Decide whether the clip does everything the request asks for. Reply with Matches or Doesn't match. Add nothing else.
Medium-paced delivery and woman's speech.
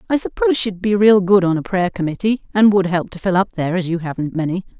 Doesn't match